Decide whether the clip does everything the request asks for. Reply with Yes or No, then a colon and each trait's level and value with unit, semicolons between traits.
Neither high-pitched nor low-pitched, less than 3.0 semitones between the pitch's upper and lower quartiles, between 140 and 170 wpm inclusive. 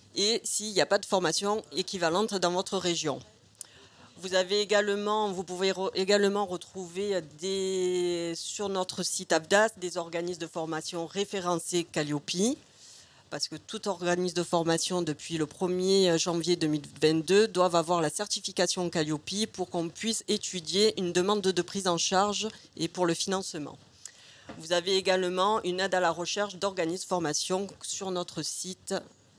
Yes: medium, 180 Hz; narrow, 2.6 semitones; average, 150 wpm